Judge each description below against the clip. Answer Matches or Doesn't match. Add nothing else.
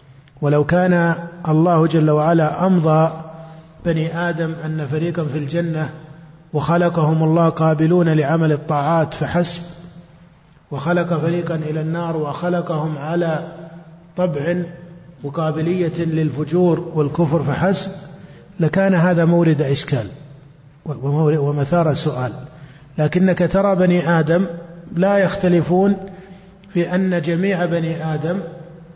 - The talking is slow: Doesn't match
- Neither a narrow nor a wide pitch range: Doesn't match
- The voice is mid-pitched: Matches